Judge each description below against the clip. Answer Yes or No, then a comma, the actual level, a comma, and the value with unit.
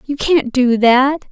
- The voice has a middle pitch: No, very high, 265 Hz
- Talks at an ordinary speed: Yes, average, 180 wpm